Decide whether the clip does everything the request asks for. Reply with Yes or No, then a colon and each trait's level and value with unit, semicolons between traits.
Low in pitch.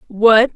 No: high, 225 Hz